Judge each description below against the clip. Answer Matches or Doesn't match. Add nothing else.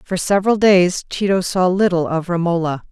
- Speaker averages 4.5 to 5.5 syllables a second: Matches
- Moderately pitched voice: Matches